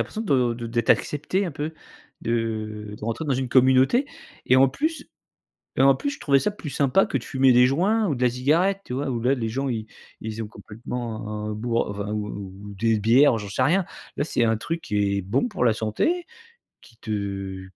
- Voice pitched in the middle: No, low, 125 Hz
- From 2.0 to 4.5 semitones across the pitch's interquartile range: No, average, 4.9 semitones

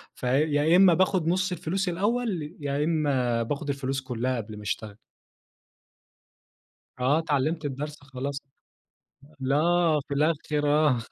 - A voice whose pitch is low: No, medium, 145 Hz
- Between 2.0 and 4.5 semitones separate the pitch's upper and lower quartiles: Yes, average, 3.7 semitones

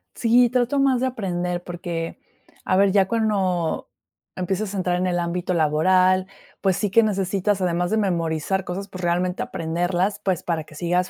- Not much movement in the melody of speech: Yes, narrow, 2.3 semitones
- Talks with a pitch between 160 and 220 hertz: Yes, medium, 185 Hz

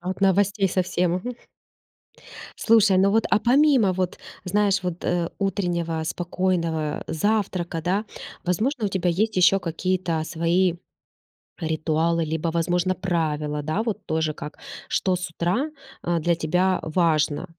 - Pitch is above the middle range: No, medium, 180 Hz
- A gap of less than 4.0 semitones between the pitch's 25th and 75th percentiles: Yes, average, 2.9 semitones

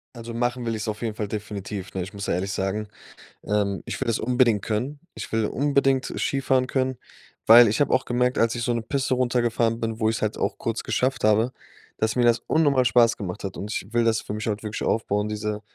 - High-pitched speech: No, low, 115 Hz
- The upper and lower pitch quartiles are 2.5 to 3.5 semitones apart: Yes, average, 2.8 semitones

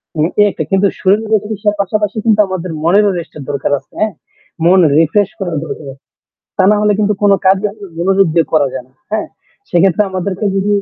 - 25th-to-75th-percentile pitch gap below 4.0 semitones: Yes, average, 3.4 semitones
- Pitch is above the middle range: Yes, high, 195 Hz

